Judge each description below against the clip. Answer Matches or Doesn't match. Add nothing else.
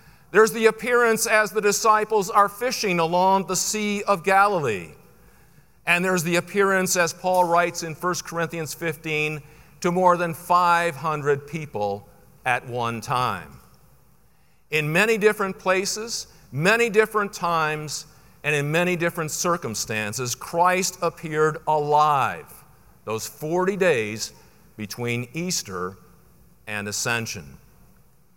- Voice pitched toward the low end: Doesn't match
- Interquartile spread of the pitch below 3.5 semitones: Doesn't match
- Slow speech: Matches